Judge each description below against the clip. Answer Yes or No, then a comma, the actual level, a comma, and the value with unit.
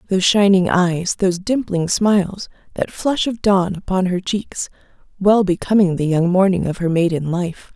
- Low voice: No, medium, 185 Hz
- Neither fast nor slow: Yes, average, 170 wpm